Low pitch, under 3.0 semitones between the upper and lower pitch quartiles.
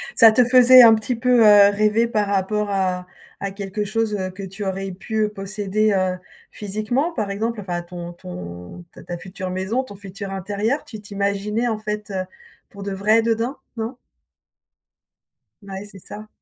No: high, 205 Hz; narrow, 2.4 semitones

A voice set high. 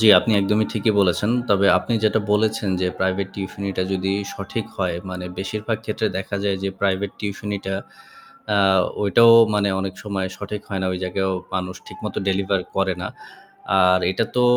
No: low, 100 Hz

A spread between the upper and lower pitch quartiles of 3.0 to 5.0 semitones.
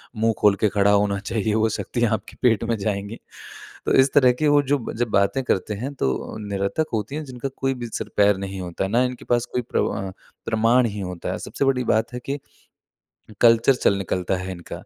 Yes: average, 3.9 semitones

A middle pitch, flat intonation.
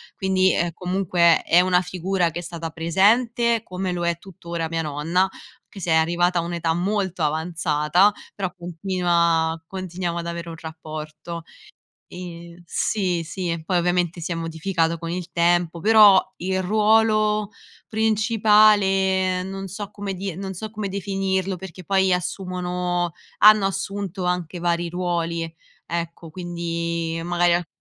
Yes: medium, 180 Hz; narrow, 2.3 semitones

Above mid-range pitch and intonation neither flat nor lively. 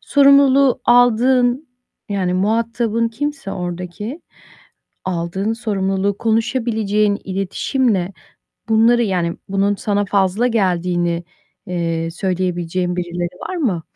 Yes: high, 200 Hz; average, 4.6 semitones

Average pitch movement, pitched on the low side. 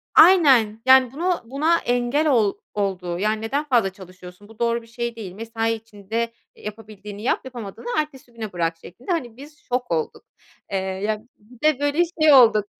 No: average, 4.2 semitones; high, 230 Hz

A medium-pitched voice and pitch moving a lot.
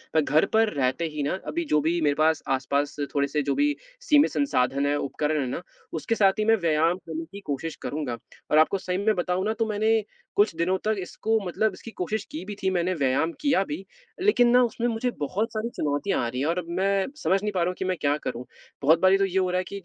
Yes: medium, 180 Hz; wide, 5.9 semitones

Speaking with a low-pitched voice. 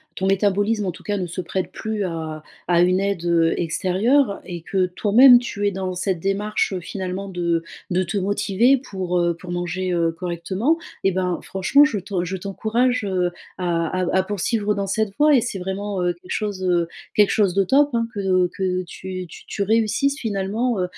No: high, 190 Hz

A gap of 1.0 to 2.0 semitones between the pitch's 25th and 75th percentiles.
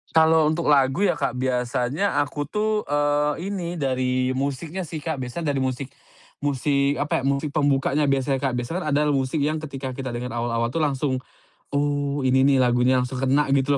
No: narrow, 2.5 semitones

